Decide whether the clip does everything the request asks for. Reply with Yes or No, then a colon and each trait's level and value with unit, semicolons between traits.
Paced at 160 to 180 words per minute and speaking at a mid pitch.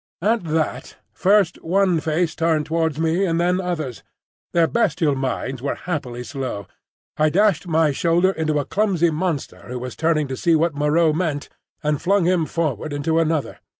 Yes: average, 170 wpm; medium, 160 Hz